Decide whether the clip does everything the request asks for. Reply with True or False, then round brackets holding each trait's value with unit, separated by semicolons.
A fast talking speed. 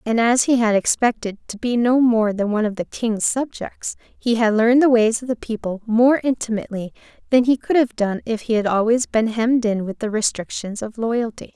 True (220 wpm)